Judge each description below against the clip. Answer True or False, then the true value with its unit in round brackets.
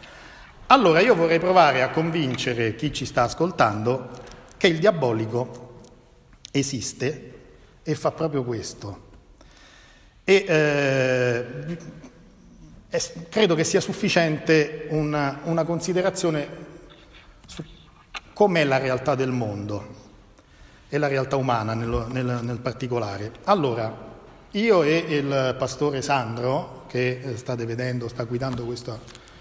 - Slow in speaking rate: True (110 wpm)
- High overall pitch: False (130 Hz)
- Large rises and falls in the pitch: False (4.3 semitones)